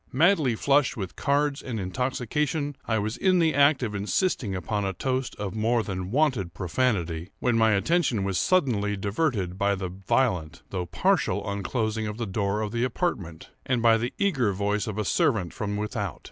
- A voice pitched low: Yes, low, 110 Hz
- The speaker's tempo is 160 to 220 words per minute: Yes, average, 180 wpm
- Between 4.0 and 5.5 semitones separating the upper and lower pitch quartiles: Yes, average, 4.9 semitones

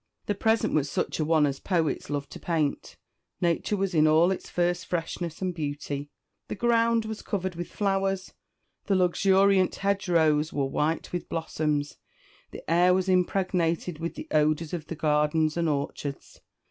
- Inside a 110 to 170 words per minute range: Yes, average, 160 wpm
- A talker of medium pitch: Yes, medium, 170 Hz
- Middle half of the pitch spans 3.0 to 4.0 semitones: Yes, average, 3.6 semitones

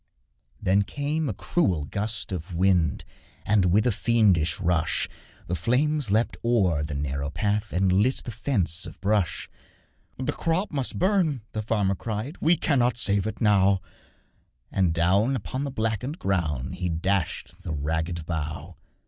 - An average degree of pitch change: No, wide, 6.0 semitones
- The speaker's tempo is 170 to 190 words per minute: No, average, 150 wpm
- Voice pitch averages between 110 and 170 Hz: No, low, 100 Hz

